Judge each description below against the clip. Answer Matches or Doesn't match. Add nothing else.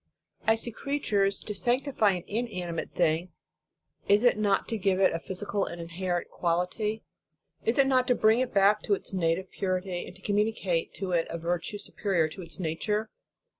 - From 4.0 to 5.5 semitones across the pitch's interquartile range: Doesn't match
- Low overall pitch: Doesn't match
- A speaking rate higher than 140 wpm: Matches